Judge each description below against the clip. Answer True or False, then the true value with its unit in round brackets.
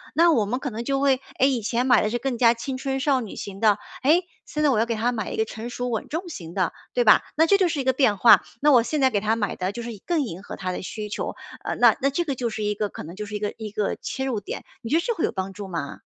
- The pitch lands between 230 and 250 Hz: True (235 Hz)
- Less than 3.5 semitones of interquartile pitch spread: False (4.5 semitones)